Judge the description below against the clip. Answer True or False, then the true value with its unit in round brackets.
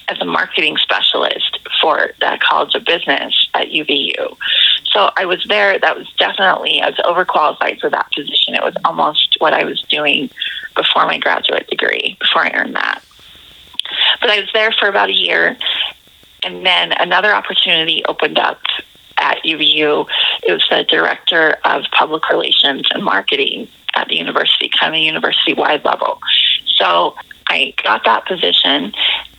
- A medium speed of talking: True (155 wpm)